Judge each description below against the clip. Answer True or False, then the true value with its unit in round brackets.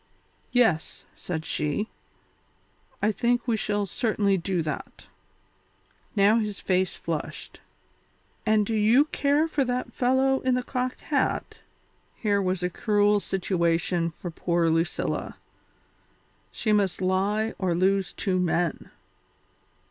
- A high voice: True (200 Hz)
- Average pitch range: True (4.3 semitones)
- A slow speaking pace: True (120 wpm)